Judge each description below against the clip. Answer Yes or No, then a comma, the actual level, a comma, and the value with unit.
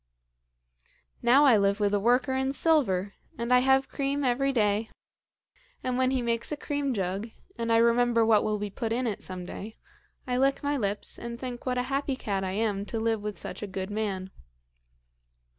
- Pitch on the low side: No, high, 235 Hz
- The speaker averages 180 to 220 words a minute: Yes, average, 195 wpm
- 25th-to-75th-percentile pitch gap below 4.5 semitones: Yes, average, 4.0 semitones